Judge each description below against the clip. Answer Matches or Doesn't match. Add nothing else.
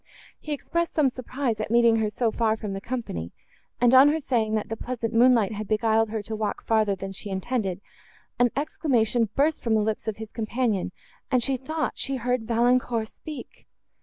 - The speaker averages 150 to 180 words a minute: Doesn't match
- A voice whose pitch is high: Matches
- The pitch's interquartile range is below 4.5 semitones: Matches